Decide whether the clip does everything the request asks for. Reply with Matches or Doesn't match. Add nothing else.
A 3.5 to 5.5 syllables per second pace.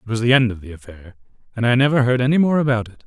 Doesn't match